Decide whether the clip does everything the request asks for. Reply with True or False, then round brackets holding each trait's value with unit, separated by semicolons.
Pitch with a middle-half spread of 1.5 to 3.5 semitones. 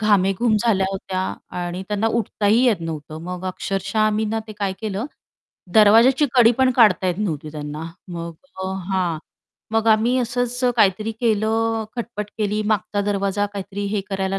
True (2.8 semitones)